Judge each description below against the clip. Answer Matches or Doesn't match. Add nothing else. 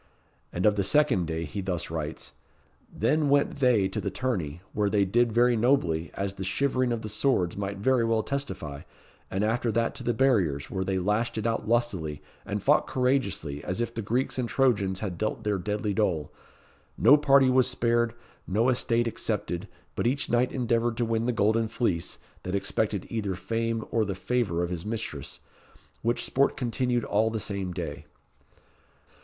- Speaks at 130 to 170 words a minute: Doesn't match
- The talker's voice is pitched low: Matches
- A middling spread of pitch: Matches